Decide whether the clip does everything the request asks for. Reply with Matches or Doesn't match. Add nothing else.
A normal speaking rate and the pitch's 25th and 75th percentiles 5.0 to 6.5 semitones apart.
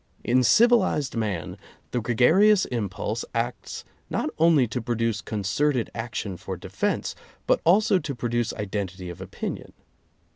Doesn't match